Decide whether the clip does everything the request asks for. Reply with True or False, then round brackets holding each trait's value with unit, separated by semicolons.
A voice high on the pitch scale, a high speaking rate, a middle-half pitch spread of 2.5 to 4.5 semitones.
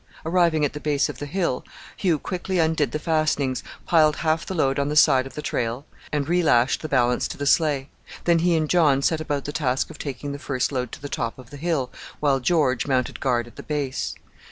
False (145 Hz; 225 wpm; 3.2 semitones)